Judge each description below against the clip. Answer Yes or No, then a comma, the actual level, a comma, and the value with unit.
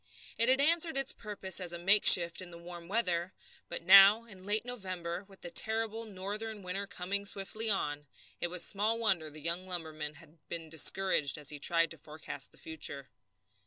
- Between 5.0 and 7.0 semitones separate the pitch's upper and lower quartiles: No, average, 3.8 semitones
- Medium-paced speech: Yes, average, 190 wpm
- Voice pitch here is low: No, medium, 185 Hz